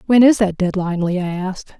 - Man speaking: No, female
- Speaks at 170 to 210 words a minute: Yes, average, 200 wpm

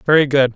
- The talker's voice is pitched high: No, low, 135 Hz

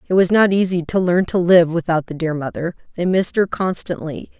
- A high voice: No, medium, 175 Hz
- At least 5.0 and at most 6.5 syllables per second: Yes, 5.5 syllables/s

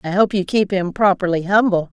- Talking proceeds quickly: Yes, fast, 210 wpm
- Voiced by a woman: Yes, female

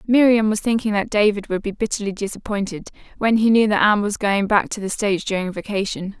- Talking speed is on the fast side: Yes, fast, 215 wpm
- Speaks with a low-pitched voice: No, high, 205 Hz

